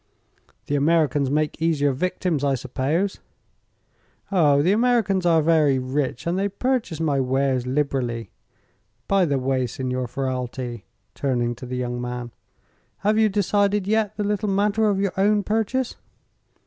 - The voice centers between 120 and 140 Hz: No, medium, 150 Hz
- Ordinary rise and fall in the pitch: No, wide, 7.4 semitones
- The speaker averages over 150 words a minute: No, average, 145 wpm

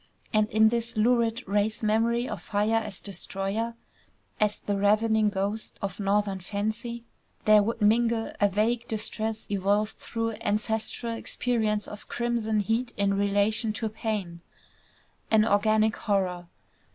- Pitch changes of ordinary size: No, narrow, 1.9 semitones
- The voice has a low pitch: No, high, 215 Hz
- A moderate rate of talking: No, slow, 130 wpm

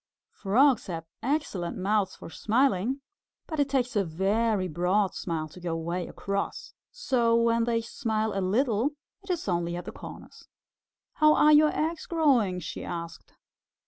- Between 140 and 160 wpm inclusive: Yes, average, 155 wpm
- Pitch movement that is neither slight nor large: No, wide, 6.8 semitones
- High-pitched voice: Yes, high, 220 Hz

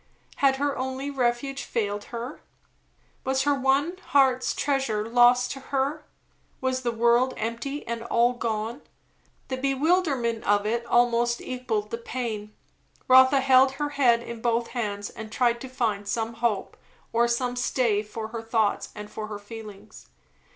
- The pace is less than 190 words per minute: Yes, average, 150 wpm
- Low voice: No, high, 240 Hz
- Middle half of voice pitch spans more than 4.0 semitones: No, average, 2.9 semitones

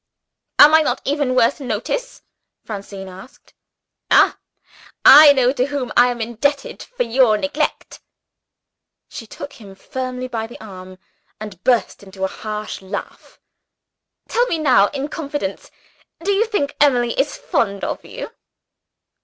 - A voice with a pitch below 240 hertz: No, very high, 250 Hz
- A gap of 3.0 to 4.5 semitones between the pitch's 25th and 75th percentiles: No, average, 5.1 semitones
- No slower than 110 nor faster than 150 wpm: Yes, average, 140 wpm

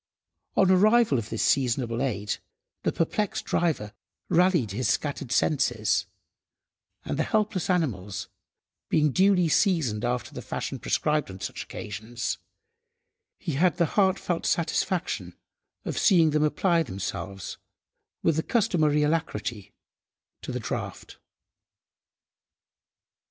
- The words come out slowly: Yes, slow, 115 wpm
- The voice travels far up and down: Yes, wide, 7.9 semitones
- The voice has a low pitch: No, medium, 150 Hz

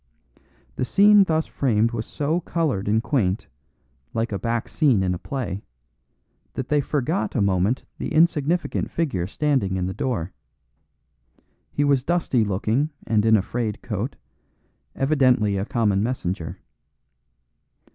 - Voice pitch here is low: Yes, low, 120 Hz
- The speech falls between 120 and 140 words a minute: Yes, slow, 135 wpm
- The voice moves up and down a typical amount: No, wide, 6.5 semitones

